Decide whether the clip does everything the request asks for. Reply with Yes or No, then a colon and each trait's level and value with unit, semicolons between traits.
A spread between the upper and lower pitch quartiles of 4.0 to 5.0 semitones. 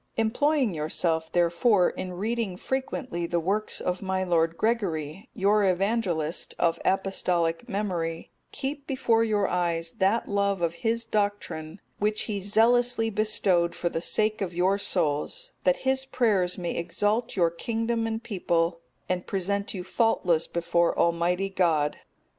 Yes: average, 4.6 semitones